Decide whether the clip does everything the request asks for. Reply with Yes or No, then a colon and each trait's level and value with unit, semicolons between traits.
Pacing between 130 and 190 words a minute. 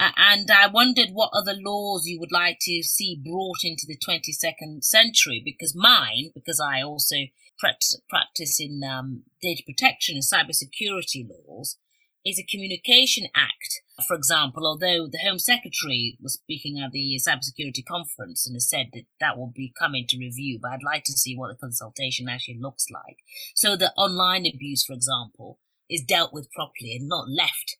Yes: average, 175 wpm